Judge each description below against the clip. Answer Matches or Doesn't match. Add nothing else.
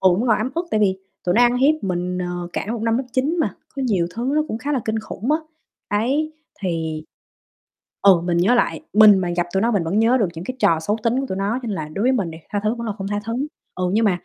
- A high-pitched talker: Matches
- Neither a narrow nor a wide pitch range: Matches